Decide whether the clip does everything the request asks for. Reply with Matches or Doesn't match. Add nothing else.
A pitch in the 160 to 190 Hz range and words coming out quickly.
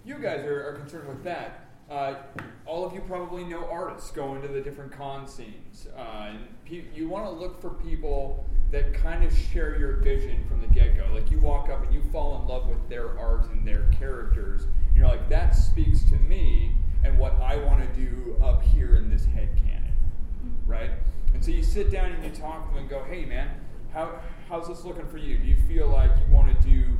Doesn't match